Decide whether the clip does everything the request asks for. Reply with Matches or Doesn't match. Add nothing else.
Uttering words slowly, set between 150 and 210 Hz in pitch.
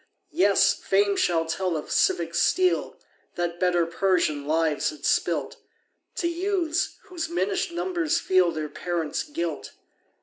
Matches